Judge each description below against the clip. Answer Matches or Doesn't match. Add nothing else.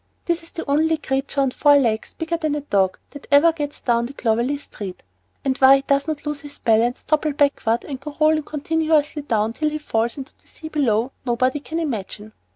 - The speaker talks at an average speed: Doesn't match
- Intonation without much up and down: Doesn't match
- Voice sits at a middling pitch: Doesn't match